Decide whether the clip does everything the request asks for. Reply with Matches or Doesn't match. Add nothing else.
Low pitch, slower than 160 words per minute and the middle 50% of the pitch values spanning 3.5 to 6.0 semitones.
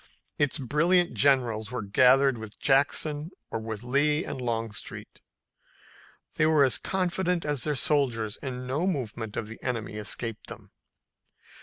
Matches